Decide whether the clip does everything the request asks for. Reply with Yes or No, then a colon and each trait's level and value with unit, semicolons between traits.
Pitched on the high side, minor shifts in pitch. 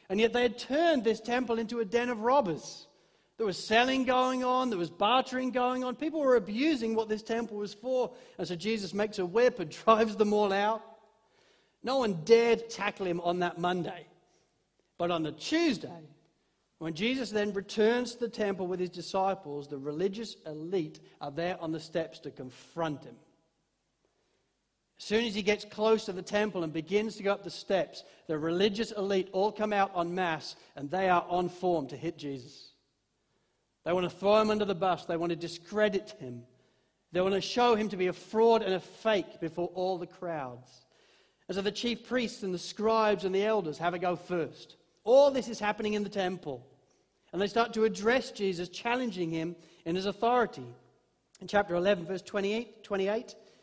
No: high, 200 Hz; average, 4.6 semitones